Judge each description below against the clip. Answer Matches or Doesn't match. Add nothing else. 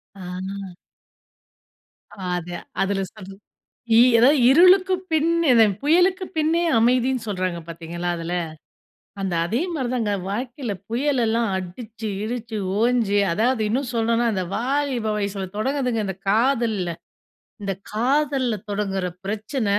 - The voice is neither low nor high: Doesn't match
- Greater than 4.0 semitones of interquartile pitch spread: Matches